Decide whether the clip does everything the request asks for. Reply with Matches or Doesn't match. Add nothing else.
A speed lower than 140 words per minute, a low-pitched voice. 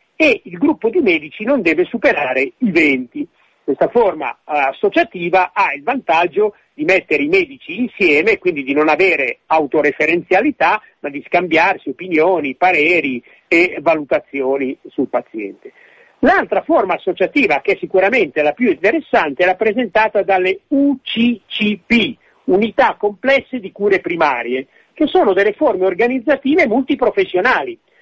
Doesn't match